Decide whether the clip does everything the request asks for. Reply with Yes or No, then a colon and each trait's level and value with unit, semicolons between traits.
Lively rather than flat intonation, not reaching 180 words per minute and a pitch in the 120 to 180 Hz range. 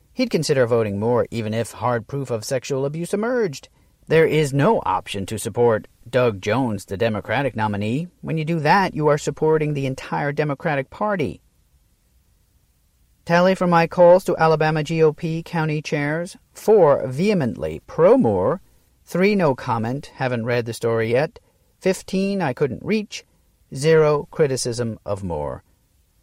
Yes: wide, 6.3 semitones; average, 145 wpm; medium, 140 Hz